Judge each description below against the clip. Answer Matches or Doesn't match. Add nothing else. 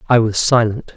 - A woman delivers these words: Doesn't match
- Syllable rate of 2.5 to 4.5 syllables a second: Doesn't match